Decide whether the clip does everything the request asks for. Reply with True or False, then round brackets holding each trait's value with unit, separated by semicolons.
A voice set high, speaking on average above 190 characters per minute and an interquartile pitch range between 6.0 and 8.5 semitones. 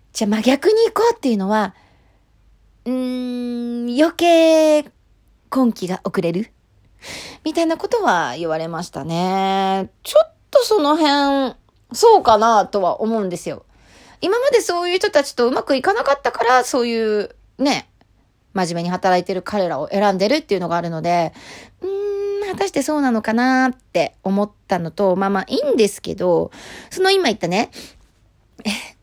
True (240 Hz; 310 characters per minute; 8.2 semitones)